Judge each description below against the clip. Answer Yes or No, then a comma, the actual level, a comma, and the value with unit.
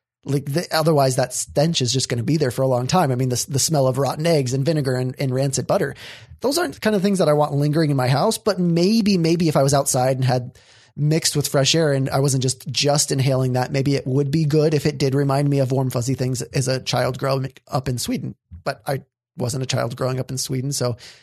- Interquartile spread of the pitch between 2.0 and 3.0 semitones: Yes, narrow, 2.5 semitones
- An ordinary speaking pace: No, fast, 265 wpm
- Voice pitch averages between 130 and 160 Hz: Yes, low, 135 Hz